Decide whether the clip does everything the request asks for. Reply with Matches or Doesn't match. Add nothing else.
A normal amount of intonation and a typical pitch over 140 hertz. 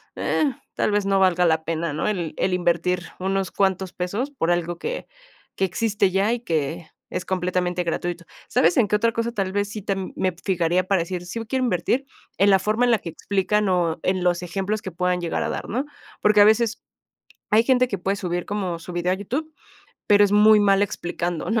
Matches